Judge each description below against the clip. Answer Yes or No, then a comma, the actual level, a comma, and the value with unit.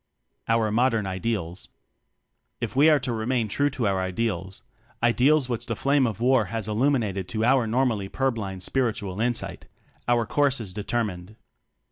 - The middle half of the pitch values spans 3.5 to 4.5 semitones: Yes, average, 4.1 semitones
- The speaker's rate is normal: Yes, average, 155 wpm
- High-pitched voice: No, low, 115 Hz